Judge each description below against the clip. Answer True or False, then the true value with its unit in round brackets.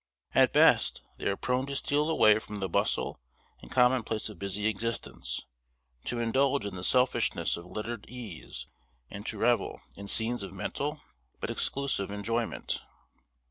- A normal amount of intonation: True (4.1 semitones)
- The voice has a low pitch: True (110 Hz)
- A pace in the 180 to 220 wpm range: False (150 wpm)